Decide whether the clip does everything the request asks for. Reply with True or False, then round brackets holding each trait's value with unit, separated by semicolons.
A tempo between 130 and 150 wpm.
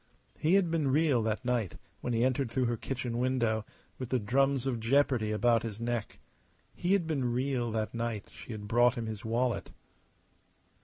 False (185 wpm)